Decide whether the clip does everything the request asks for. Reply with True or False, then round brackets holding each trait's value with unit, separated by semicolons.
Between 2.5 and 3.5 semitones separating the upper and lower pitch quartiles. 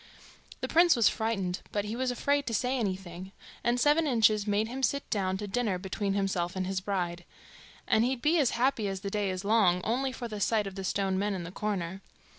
False (4.1 semitones)